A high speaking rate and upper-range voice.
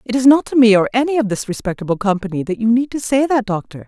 Yes: fast, 280 wpm; high, 230 Hz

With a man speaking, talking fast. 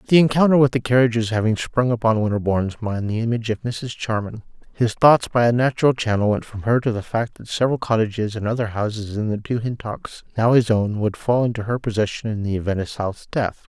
Yes: male; fast, 225 wpm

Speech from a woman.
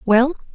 Yes: female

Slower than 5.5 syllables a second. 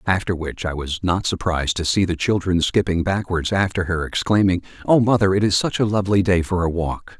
No: 5.6 syllables/s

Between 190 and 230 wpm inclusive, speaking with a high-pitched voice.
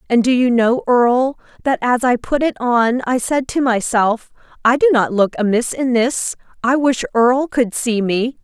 Yes: average, 200 wpm; high, 245 Hz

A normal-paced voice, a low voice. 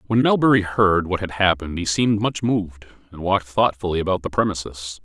Yes: average, 190 wpm; very low, 95 Hz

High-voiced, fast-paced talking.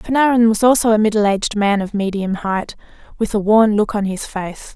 Yes: high, 210 Hz; fast, 215 wpm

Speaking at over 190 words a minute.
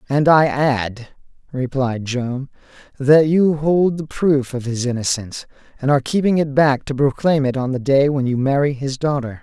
No: average, 185 wpm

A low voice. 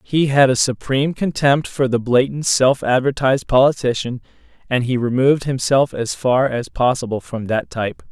Yes: low, 130 Hz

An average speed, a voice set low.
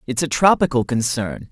Yes: average, 160 wpm; low, 130 Hz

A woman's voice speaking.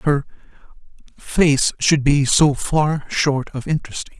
No: male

